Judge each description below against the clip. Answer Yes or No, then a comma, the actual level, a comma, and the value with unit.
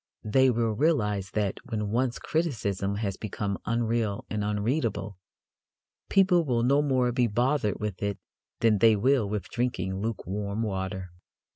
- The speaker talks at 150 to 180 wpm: No, average, 140 wpm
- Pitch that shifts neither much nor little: Yes, average, 3.6 semitones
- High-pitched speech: No, low, 110 Hz